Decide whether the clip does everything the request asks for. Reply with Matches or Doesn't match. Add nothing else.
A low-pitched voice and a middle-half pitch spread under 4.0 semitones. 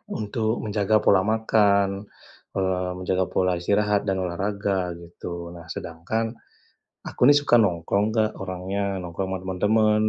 Matches